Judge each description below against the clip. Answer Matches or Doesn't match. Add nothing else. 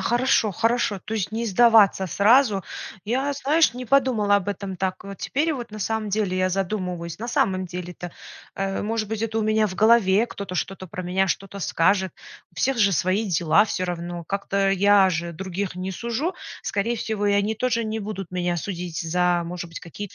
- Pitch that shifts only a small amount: Doesn't match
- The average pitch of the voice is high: Matches